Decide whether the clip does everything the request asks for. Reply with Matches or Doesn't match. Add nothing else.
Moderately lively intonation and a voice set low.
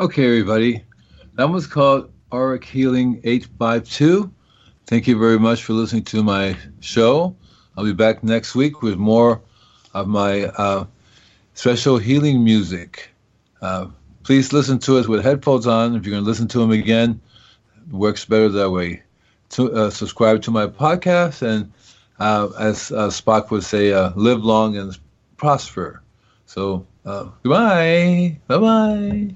Matches